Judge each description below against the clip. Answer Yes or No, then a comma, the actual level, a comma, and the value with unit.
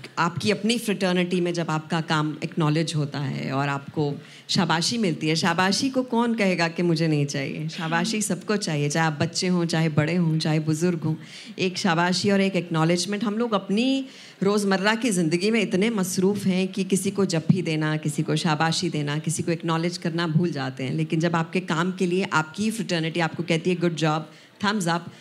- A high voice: No, medium, 170 Hz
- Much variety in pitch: No, average, 3.4 semitones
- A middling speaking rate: No, fast, 200 wpm